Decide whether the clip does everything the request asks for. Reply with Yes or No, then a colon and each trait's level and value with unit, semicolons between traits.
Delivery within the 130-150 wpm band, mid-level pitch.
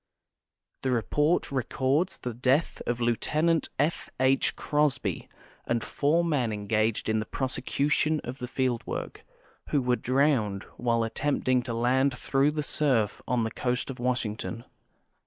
No: average, 145 wpm; low, 125 Hz